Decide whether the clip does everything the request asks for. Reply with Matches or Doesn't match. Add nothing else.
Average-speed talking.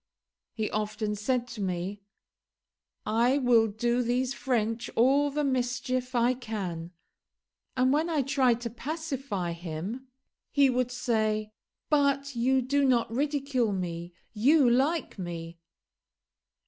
Doesn't match